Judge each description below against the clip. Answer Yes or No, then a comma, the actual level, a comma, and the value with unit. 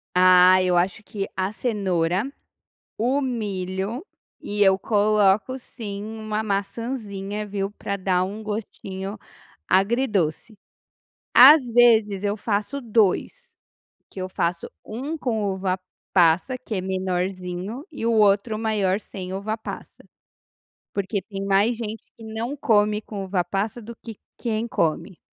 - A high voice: Yes, high, 205 Hz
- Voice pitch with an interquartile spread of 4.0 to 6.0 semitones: No, average, 2.9 semitones